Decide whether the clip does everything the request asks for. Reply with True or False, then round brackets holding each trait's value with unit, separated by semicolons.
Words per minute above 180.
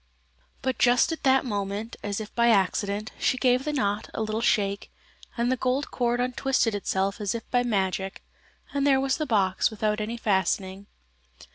False (175 wpm)